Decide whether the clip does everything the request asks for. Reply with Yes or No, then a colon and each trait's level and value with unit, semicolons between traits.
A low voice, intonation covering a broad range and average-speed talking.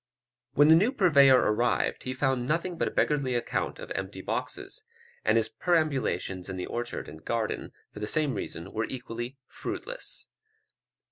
Yes: low, 125 Hz; wide, 5.7 semitones; average, 160 wpm